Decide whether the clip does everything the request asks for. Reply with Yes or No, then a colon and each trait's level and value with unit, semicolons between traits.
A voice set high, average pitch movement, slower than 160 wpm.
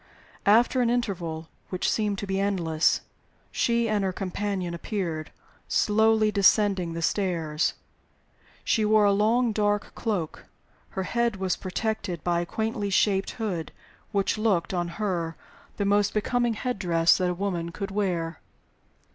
Yes: high, 200 Hz; average, 3.5 semitones; average, 145 wpm